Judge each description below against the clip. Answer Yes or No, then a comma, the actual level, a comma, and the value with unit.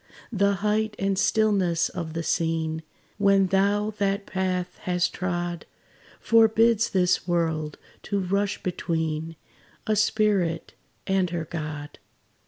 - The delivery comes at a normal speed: No, slow, 115 wpm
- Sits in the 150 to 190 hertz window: Yes, medium, 185 Hz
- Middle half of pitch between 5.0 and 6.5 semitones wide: No, average, 3.3 semitones